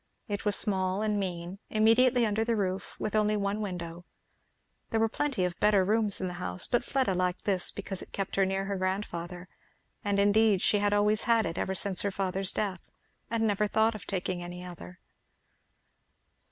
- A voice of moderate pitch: No, high, 200 Hz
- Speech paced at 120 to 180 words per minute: No, average, 190 wpm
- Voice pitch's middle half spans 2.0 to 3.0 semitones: Yes, narrow, 2.6 semitones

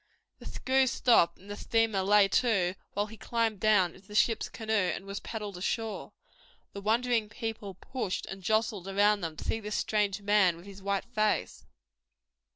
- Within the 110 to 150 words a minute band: No, average, 175 wpm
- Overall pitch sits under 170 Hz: No, high, 210 Hz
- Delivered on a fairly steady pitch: Yes, narrow, 2.3 semitones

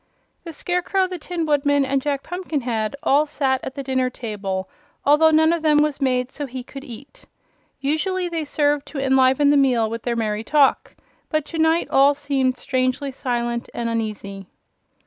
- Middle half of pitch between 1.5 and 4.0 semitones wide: Yes, average, 3.3 semitones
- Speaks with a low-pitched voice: No, very high, 275 Hz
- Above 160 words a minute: Yes, average, 175 wpm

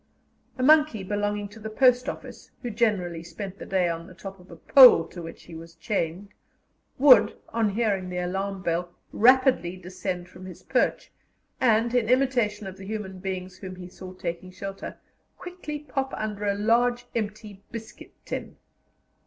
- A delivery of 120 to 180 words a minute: Yes, average, 170 wpm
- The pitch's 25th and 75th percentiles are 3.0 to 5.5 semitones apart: Yes, average, 4.0 semitones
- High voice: Yes, high, 200 Hz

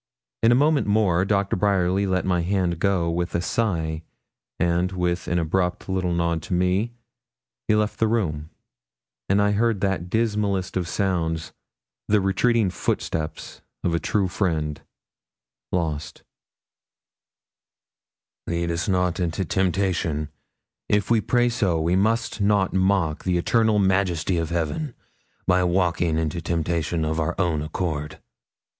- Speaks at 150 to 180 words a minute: No, average, 140 wpm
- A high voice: No, very low, 90 Hz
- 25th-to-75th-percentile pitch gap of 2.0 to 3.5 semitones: Yes, average, 3.1 semitones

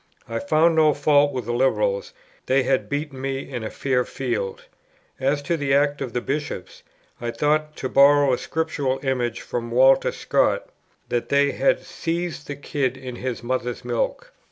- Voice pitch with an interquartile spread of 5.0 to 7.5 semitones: No, average, 2.7 semitones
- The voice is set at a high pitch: No, low, 135 Hz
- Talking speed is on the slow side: No, average, 175 wpm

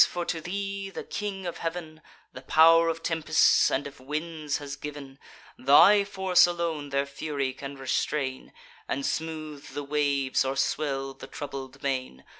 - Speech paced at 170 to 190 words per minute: No, average, 155 wpm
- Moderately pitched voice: Yes, medium, 150 Hz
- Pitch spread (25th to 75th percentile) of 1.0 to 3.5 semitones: Yes, average, 3.2 semitones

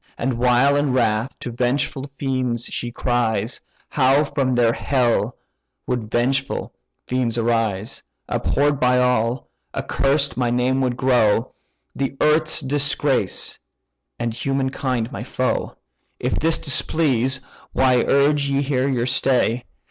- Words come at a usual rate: No, slow, 125 wpm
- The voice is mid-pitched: No, low, 130 Hz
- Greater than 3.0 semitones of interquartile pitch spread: No, narrow, 2.5 semitones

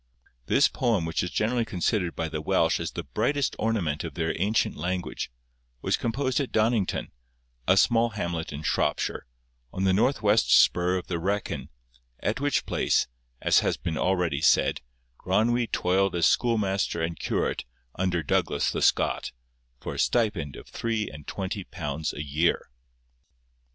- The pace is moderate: Yes, average, 155 wpm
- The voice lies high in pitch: No, very low, 95 Hz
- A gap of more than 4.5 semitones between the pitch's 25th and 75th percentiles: Yes, average, 5.1 semitones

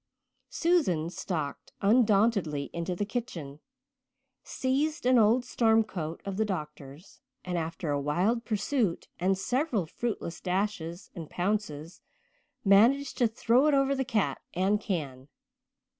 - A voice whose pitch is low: No, high, 200 Hz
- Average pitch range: No, wide, 6.1 semitones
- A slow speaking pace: Yes, slow, 130 wpm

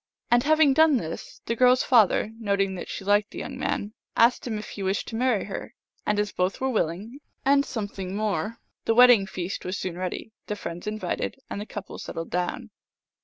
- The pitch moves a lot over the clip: No, average, 4.1 semitones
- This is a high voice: Yes, high, 210 Hz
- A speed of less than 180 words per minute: No, fast, 205 wpm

